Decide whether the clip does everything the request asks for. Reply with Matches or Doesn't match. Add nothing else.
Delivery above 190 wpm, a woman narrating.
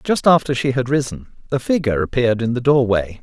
Doesn't match